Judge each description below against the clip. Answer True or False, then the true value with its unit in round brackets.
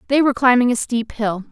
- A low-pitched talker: False (240 Hz)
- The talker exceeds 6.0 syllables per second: True (6.2 syllables/s)